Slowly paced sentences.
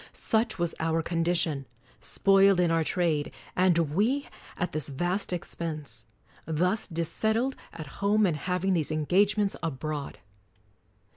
Yes: slow, 125 wpm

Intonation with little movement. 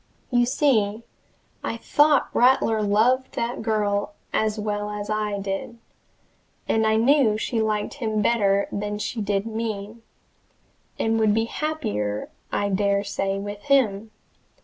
Yes: narrow, 2.2 semitones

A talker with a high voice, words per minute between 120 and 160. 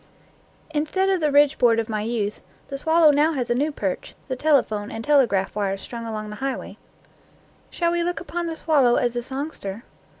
No: very high, 265 Hz; fast, 205 wpm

